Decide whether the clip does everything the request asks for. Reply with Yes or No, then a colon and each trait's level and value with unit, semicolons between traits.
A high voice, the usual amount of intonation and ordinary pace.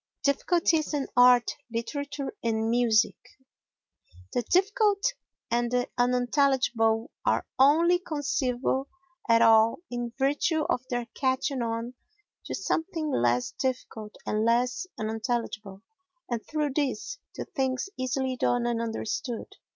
No: very high, 250 Hz; average, 3.7 semitones; slow, 115 wpm